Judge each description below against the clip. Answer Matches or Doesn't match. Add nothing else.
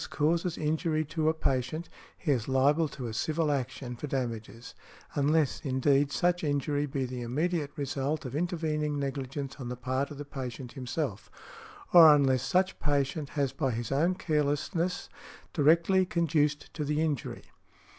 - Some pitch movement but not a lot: Matches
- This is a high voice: Doesn't match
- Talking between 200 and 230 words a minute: Doesn't match